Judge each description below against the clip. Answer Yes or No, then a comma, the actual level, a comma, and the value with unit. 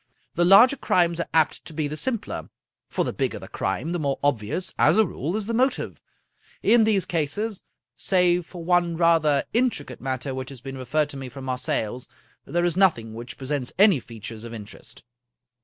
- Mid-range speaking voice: Yes, medium, 155 Hz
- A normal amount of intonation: No, wide, 5.7 semitones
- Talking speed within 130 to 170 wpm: No, average, 190 wpm